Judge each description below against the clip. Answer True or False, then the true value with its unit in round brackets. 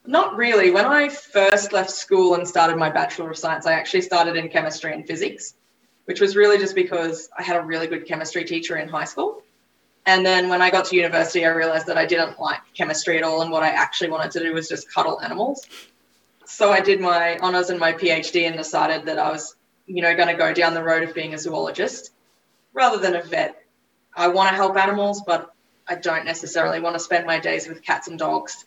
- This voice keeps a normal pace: False (230 wpm)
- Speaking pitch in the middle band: True (170 Hz)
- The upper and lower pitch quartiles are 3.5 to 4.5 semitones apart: False (2.8 semitones)